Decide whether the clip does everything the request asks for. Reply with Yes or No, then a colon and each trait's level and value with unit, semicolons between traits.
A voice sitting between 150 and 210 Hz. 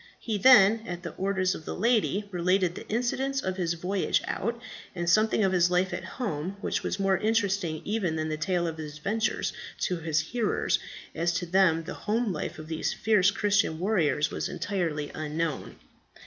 Yes: medium, 185 Hz